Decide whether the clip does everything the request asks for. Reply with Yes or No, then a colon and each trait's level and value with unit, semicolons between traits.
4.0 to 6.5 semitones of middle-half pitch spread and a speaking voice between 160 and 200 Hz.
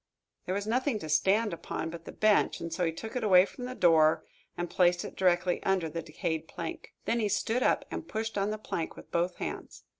Yes: average, 4.3 semitones; medium, 185 Hz